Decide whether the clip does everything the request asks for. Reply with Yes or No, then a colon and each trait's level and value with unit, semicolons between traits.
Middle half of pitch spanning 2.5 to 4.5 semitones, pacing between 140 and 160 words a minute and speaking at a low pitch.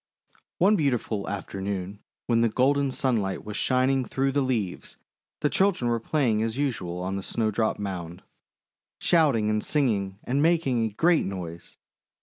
No: wide, 5.5 semitones; average, 145 wpm; low, 115 Hz